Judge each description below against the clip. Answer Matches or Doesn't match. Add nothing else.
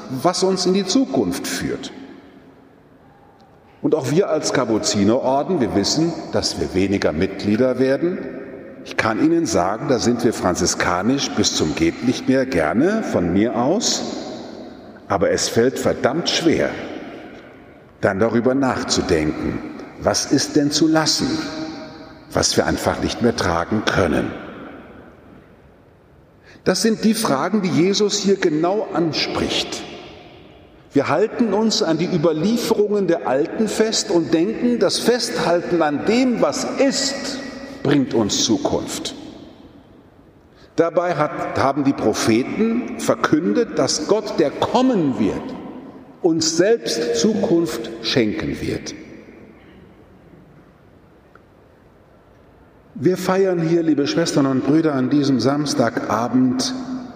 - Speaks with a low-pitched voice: Doesn't match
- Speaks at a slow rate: Matches